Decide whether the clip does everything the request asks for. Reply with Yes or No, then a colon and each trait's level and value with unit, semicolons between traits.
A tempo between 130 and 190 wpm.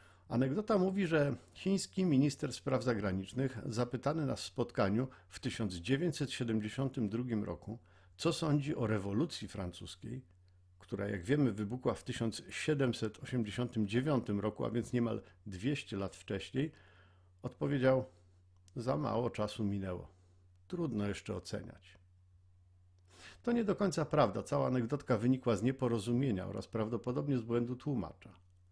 No: average, 115 wpm